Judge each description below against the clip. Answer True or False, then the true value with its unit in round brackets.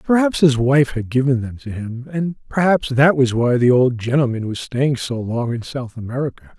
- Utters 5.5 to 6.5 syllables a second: False (4.9 syllables/s)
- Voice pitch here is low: True (130 Hz)